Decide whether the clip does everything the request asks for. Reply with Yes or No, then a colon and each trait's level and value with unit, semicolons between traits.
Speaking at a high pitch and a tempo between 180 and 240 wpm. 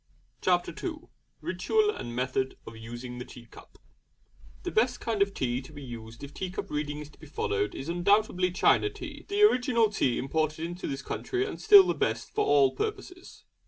No: medium, 160 Hz; average, 190 wpm